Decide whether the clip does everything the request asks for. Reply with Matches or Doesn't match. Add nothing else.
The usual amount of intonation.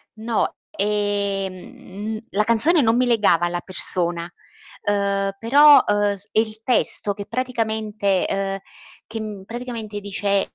Doesn't match